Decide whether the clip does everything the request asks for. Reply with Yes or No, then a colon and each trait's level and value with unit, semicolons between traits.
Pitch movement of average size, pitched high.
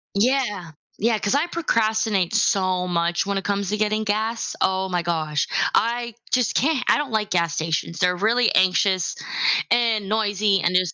Yes: average, 3.8 semitones; high, 205 Hz